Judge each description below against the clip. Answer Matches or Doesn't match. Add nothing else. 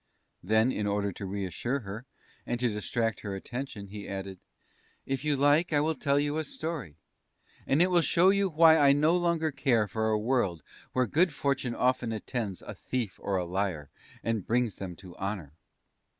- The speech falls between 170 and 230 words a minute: Matches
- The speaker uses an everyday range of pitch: Doesn't match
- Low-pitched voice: Matches